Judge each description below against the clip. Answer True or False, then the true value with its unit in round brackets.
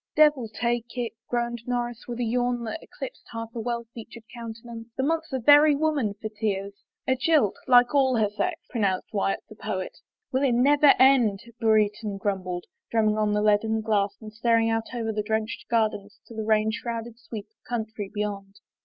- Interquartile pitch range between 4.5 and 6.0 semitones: False (2.4 semitones)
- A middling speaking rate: False (215 wpm)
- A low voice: False (225 Hz)